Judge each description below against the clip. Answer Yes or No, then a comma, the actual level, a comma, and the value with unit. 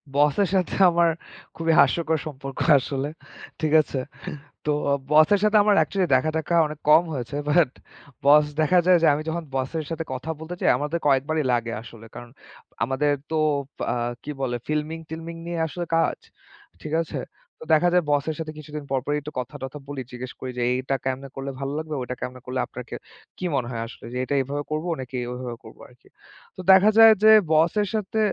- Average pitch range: Yes, average, 3.7 semitones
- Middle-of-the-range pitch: Yes, medium, 150 Hz